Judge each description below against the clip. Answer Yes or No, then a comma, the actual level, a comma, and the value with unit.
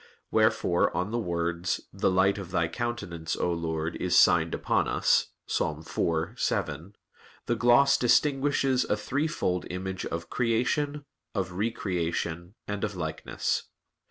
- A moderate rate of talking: No, slow, 130 wpm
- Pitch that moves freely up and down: Yes, wide, 5.7 semitones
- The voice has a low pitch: Yes, very low, 95 Hz